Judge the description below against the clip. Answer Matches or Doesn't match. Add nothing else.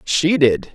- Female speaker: Doesn't match